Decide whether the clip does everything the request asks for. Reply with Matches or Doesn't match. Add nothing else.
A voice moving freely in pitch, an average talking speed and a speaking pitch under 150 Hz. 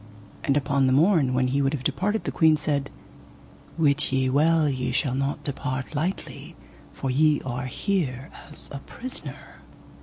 Doesn't match